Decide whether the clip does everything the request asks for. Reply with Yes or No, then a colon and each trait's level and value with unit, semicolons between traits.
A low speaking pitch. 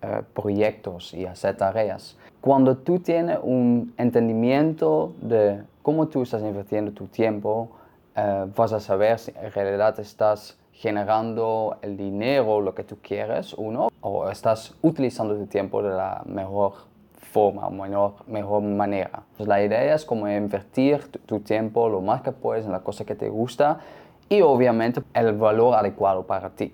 Yes: low, 110 Hz